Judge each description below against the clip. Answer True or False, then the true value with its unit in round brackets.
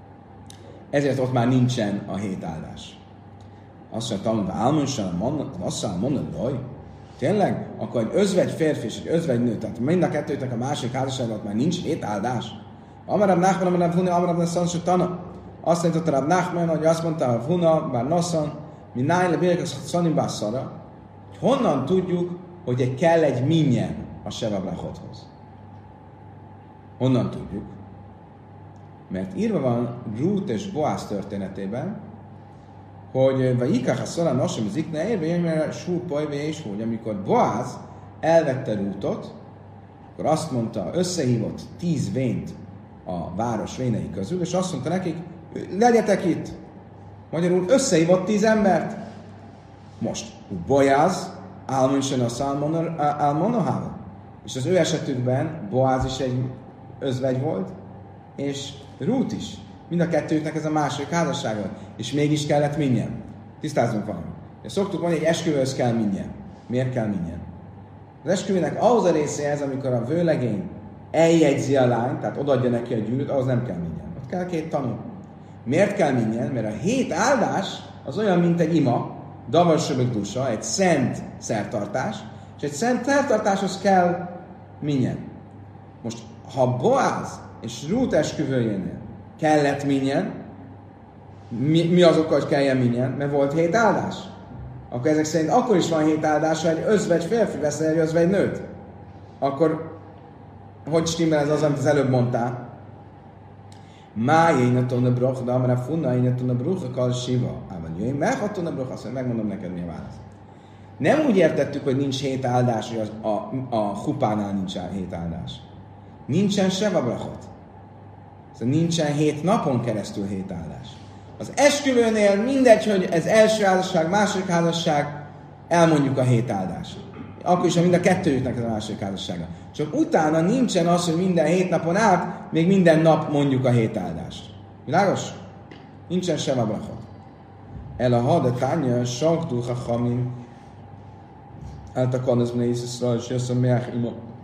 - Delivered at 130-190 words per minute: True (135 wpm)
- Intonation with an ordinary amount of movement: False (6.7 semitones)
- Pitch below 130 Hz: False (135 Hz)